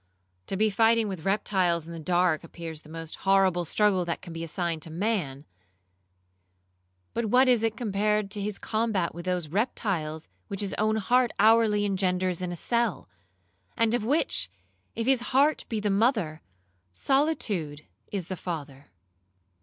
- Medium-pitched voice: No, high, 195 Hz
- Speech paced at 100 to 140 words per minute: No, average, 160 wpm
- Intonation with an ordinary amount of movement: Yes, average, 4.7 semitones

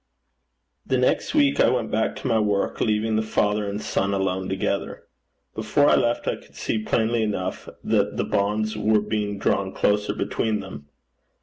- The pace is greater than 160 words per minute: Yes, average, 175 wpm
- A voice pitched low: Yes, low, 105 Hz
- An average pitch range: No, narrow, 1.8 semitones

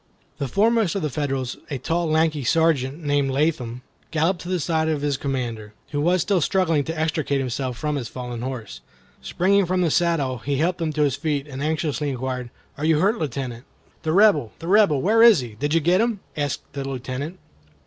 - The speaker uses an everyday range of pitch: Yes, average, 4.1 semitones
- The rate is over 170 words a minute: Yes, average, 200 wpm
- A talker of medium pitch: Yes, medium, 150 Hz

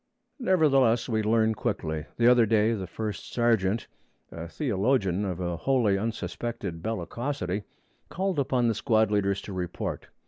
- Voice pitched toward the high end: No, low, 110 Hz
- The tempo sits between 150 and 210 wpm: No, average, 140 wpm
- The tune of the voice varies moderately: Yes, average, 3.7 semitones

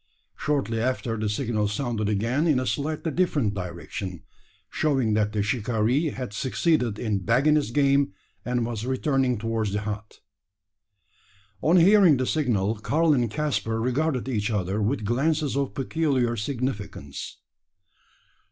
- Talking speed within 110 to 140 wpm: Yes, slow, 135 wpm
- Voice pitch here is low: Yes, low, 125 Hz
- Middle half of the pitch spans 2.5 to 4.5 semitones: No, average, 4.9 semitones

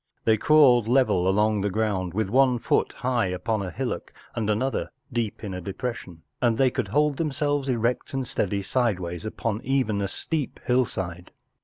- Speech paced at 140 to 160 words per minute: No, average, 175 wpm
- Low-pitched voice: Yes, low, 110 Hz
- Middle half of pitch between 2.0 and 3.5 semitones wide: No, average, 4.8 semitones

